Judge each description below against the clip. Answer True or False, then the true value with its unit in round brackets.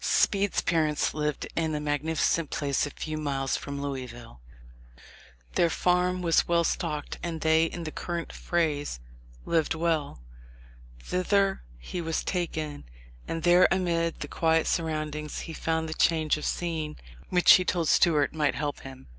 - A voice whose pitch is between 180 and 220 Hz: False (160 Hz)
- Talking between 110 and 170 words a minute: True (150 wpm)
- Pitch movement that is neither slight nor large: False (2.3 semitones)